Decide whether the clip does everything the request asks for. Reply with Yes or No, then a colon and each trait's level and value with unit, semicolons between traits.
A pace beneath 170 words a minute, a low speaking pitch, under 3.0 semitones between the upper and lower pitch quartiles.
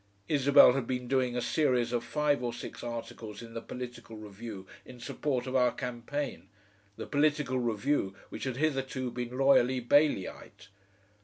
Yes: average, 155 wpm; low, 125 Hz; narrow, 2.4 semitones